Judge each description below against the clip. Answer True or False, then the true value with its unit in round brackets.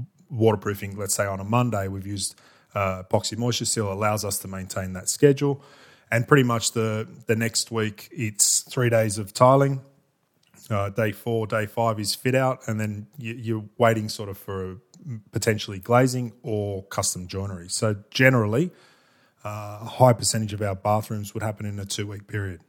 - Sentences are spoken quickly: False (180 wpm)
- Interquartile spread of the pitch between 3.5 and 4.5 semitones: False (2.9 semitones)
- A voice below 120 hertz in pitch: True (110 Hz)